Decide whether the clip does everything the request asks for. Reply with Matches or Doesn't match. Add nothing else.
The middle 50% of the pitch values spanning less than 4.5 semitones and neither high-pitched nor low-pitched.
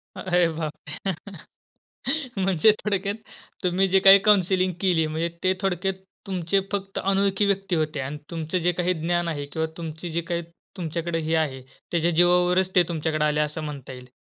Matches